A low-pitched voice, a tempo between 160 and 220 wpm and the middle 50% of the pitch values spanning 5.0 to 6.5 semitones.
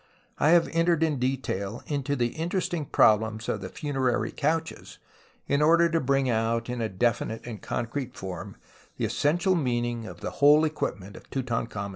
Yes: low, 130 Hz; average, 170 wpm; average, 5.3 semitones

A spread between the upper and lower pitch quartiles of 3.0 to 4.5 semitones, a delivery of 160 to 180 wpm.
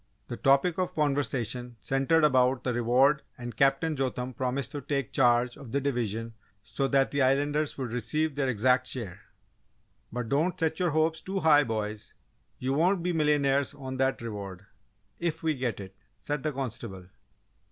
Yes: average, 3.4 semitones; average, 165 wpm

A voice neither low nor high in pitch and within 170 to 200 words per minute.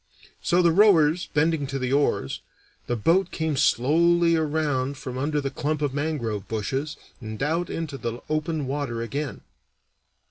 No: medium, 145 Hz; average, 150 wpm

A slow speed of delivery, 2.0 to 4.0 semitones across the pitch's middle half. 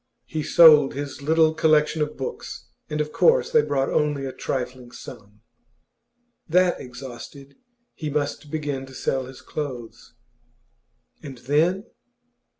Yes: slow, 130 wpm; average, 2.9 semitones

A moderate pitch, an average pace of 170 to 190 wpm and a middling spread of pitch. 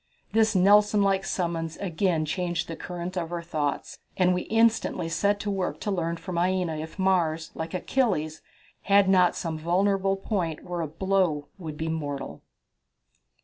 No: medium, 180 Hz; average, 160 wpm; average, 3.2 semitones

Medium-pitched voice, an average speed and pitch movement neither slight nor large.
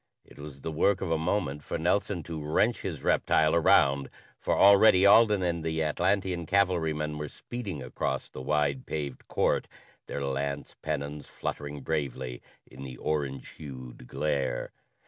No: very low, 75 Hz; average, 150 wpm; average, 3.9 semitones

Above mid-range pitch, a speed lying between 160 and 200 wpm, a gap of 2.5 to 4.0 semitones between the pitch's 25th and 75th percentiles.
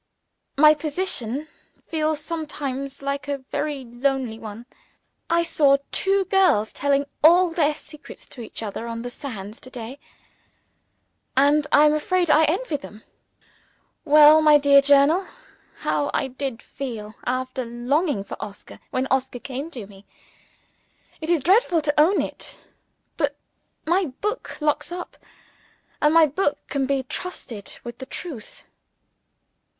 No: very high, 285 Hz; average, 140 wpm; average, 3.6 semitones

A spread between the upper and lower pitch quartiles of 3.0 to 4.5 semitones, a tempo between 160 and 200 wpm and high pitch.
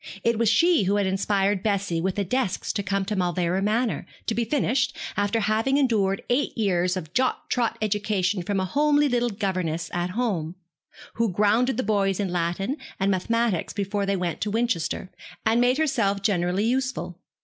Yes: average, 3.8 semitones; average, 180 wpm; high, 205 Hz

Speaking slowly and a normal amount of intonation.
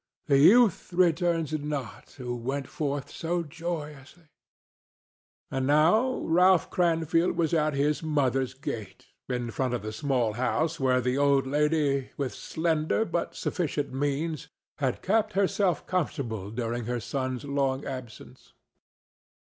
Yes: slow, 130 wpm; average, 4.2 semitones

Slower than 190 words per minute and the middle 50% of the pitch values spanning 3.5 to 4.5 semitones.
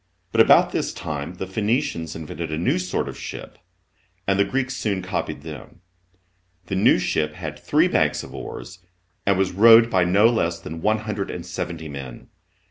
Yes: average, 180 wpm; average, 4.0 semitones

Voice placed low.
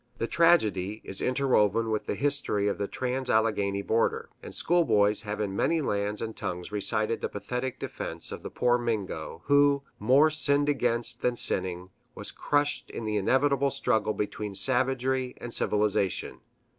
Yes: low, 115 Hz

